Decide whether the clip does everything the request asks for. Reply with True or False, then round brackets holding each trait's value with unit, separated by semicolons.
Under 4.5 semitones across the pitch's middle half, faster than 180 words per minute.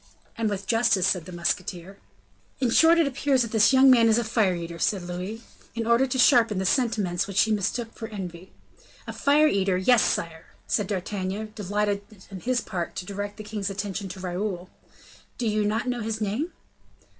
True (3.6 semitones; 190 wpm)